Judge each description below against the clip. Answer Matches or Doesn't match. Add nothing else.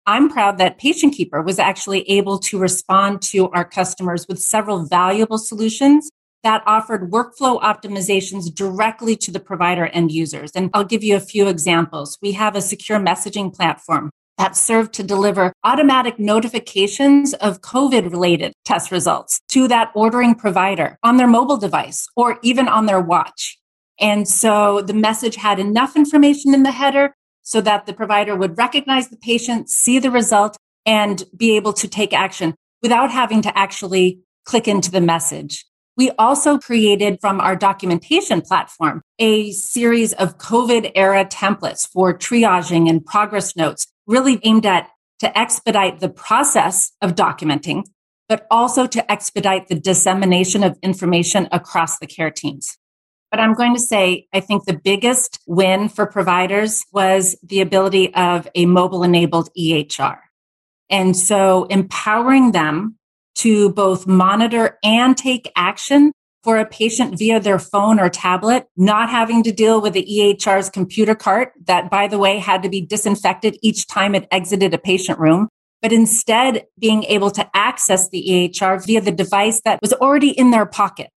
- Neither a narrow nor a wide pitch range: Matches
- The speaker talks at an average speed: Matches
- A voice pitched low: Doesn't match